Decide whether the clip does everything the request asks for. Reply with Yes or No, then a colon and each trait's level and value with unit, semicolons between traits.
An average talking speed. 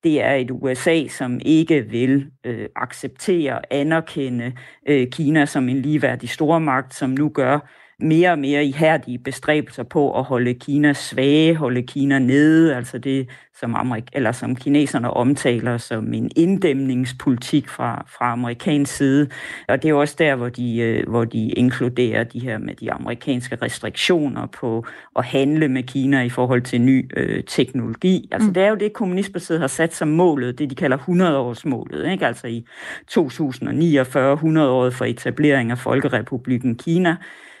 Yes: average, 160 wpm